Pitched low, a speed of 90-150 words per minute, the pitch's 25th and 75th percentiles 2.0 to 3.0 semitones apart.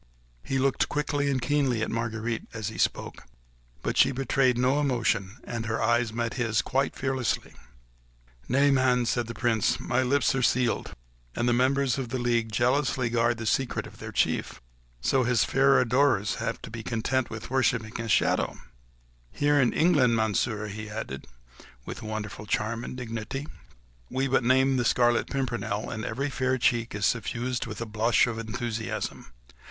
No: low, 120 Hz; average, 170 wpm; average, 2.7 semitones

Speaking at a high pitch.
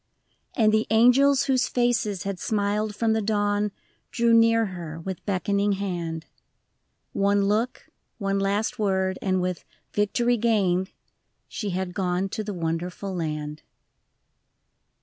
Yes: high, 200 Hz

